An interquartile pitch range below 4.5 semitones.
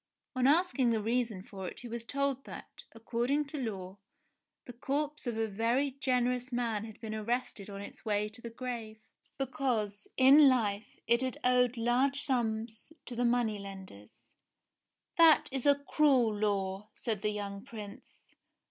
Yes: average, 3.5 semitones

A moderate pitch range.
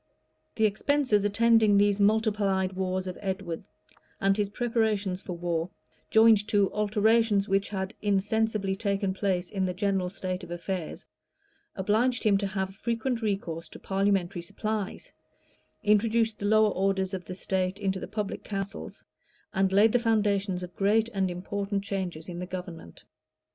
No: narrow, 2.2 semitones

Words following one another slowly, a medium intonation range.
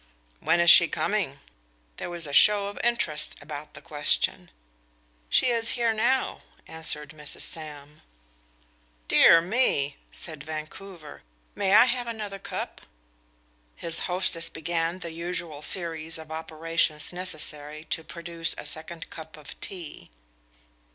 Yes: slow, 130 wpm; average, 3.2 semitones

